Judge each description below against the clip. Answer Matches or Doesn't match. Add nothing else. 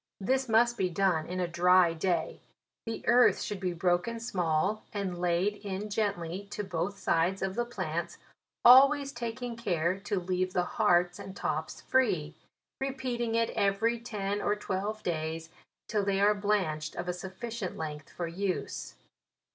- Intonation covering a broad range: Doesn't match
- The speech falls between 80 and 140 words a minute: Doesn't match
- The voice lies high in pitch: Matches